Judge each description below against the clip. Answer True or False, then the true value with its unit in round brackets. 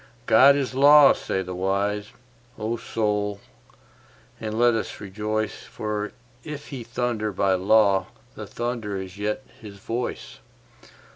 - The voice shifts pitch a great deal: False (3.0 semitones)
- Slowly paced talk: True (125 wpm)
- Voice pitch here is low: True (110 Hz)